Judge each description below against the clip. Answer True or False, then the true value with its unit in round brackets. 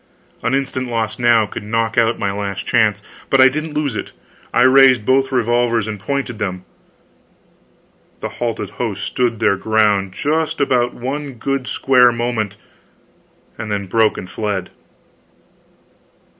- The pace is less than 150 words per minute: True (140 wpm)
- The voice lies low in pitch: True (115 Hz)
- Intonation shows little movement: False (3.8 semitones)